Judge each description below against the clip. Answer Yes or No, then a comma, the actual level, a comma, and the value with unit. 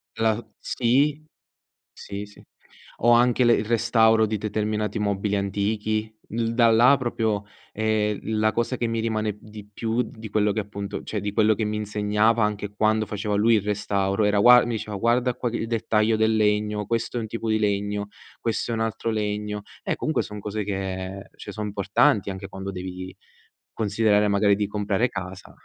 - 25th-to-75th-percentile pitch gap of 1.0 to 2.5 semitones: Yes, narrow, 1.7 semitones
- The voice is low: Yes, low, 105 Hz